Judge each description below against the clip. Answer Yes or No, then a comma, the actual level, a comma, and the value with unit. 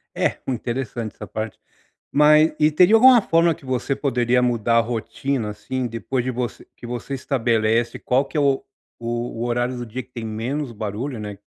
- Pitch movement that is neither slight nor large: Yes, average, 3.1 semitones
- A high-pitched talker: No, low, 125 Hz